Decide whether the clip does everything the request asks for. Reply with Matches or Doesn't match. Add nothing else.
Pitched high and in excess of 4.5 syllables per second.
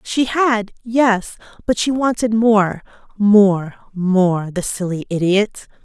Doesn't match